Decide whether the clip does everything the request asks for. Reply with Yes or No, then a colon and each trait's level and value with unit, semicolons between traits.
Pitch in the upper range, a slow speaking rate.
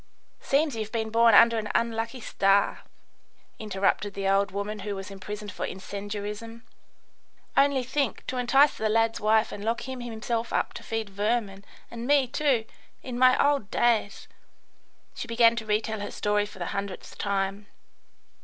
No: high, 220 Hz; average, 165 wpm